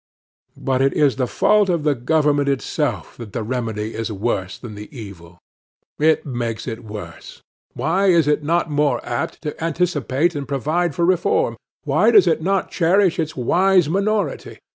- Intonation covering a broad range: Yes, wide, 6.4 semitones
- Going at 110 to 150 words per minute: No, average, 165 wpm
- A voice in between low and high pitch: Yes, medium, 145 Hz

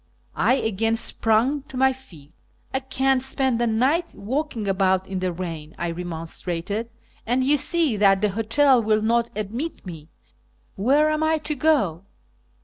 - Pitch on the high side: Yes, high, 225 Hz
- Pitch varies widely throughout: Yes, wide, 5.8 semitones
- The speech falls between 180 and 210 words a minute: No, average, 165 wpm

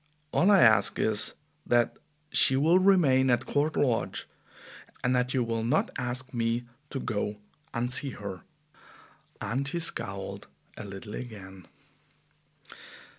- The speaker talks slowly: Yes, slow, 130 wpm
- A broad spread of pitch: No, average, 3.6 semitones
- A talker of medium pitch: No, low, 120 Hz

